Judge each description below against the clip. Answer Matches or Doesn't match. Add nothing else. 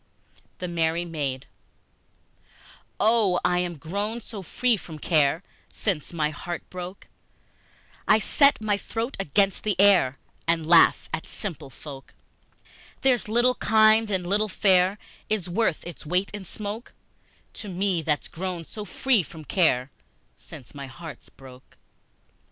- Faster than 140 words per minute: Doesn't match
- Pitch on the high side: Doesn't match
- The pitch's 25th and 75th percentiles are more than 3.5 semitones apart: Matches